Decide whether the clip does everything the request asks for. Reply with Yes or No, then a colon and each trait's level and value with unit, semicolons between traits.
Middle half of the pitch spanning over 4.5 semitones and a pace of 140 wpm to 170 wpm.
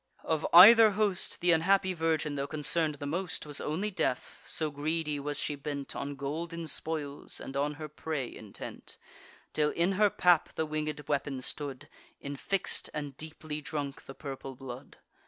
No: average, 2.8 semitones; average, 160 wpm